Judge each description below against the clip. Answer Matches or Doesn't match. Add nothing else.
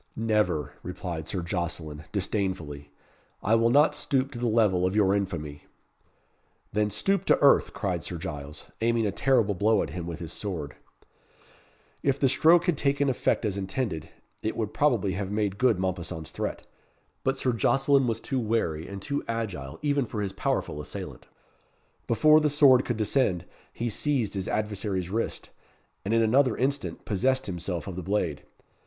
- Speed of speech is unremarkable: Matches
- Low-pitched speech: Matches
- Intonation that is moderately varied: Doesn't match